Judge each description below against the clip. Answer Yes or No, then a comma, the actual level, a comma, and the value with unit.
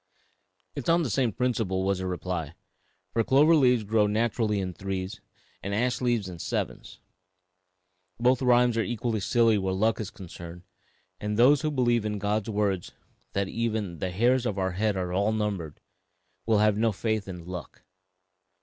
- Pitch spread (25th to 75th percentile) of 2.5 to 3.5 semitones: No, average, 3.9 semitones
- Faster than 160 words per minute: Yes, average, 170 wpm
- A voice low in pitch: Yes, low, 105 Hz